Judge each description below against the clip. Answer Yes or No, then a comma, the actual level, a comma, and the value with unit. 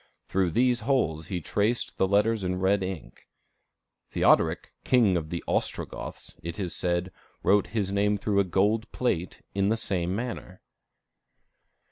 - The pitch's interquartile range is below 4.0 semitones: Yes, average, 3.2 semitones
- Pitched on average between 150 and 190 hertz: No, low, 100 Hz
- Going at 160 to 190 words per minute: No, average, 145 wpm